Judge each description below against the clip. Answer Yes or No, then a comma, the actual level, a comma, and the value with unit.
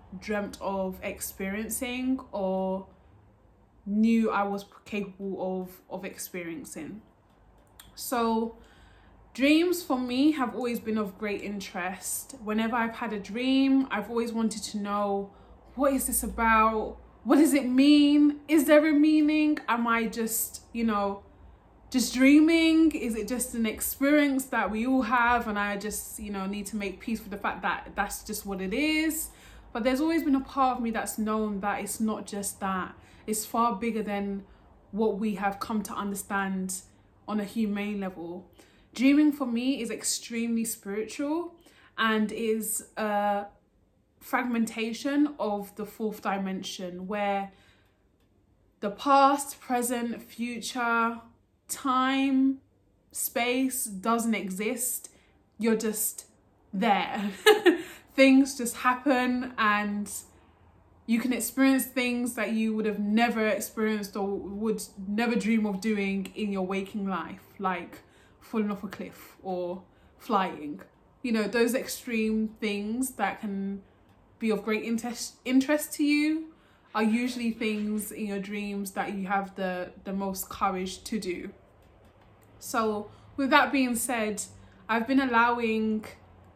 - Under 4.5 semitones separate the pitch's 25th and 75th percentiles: Yes, average, 3.9 semitones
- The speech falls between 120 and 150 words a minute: Yes, average, 140 wpm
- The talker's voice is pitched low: No, high, 220 Hz